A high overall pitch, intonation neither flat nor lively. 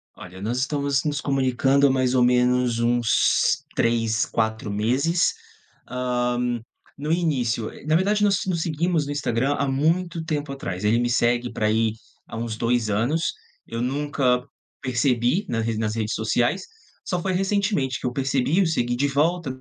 No: low, 130 Hz; average, 4.3 semitones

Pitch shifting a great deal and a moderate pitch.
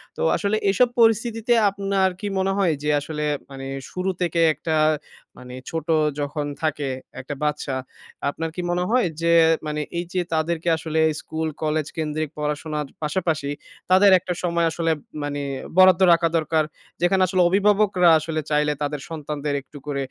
No: average, 3.7 semitones; medium, 160 Hz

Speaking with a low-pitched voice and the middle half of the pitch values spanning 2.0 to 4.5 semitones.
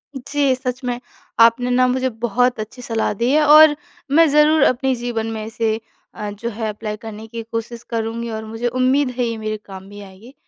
No: high, 235 Hz; narrow, 2.6 semitones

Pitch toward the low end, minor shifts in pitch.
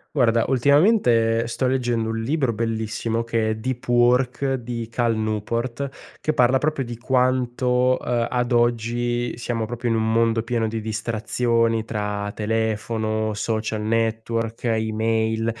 Yes: low, 115 Hz; narrow, 1.6 semitones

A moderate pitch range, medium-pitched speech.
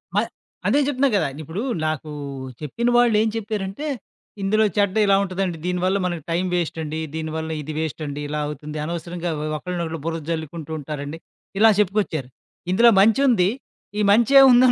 Yes: average, 5.0 semitones; medium, 180 Hz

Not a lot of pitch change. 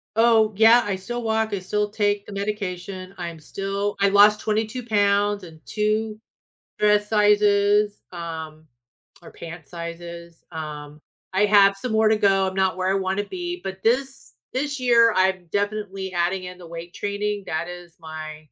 No: average, 3.1 semitones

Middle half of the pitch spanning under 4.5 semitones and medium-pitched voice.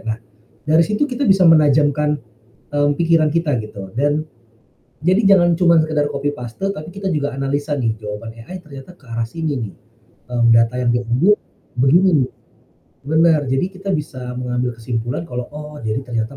No: average, 5.0 semitones; medium, 145 Hz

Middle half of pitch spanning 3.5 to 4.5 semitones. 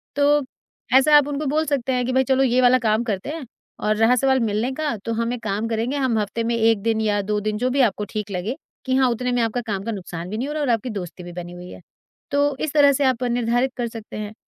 Yes: average, 3.8 semitones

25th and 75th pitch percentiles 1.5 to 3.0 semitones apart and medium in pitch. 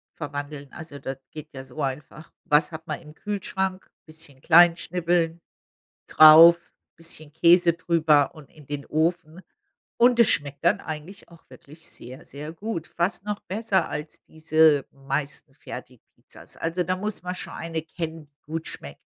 Yes: average, 2.7 semitones; medium, 160 Hz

